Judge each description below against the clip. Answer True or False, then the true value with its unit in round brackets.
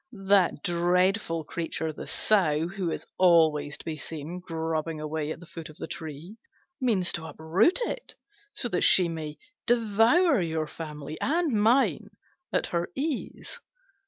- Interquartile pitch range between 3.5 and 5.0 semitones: True (4.6 semitones)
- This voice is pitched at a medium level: True (170 Hz)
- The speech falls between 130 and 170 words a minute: True (145 wpm)